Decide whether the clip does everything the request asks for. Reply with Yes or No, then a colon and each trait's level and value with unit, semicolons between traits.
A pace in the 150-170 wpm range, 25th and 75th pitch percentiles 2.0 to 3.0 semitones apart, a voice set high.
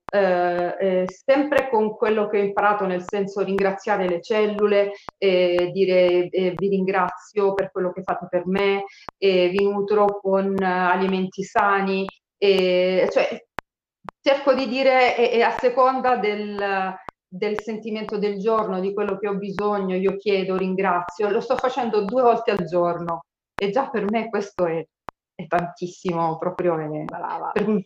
Yes: average, 155 wpm; narrow, 2.4 semitones; high, 195 Hz